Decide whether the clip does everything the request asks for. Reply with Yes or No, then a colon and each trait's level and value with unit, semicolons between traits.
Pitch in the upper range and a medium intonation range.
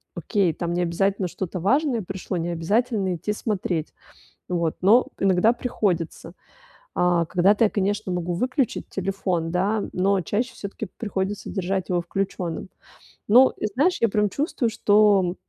Yes: high, 195 Hz; average, 3.3 semitones